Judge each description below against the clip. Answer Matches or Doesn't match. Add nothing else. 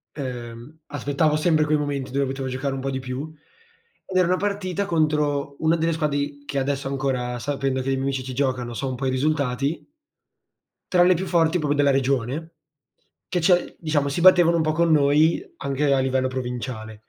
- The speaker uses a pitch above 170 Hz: Doesn't match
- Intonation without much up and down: Doesn't match